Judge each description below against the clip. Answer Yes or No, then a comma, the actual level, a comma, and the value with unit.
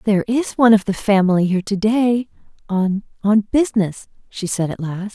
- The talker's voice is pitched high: Yes, high, 205 Hz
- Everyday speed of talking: Yes, average, 175 wpm